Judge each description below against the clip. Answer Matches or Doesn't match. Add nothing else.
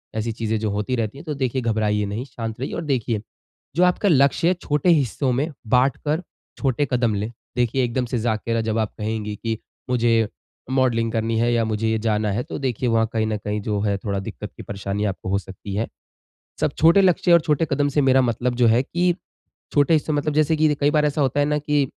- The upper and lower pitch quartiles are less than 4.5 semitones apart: Doesn't match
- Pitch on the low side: Matches